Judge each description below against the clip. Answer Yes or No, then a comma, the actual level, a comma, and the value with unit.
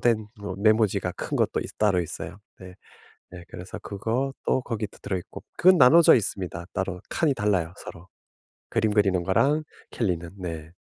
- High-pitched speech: No, low, 100 Hz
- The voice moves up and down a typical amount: Yes, average, 4.0 semitones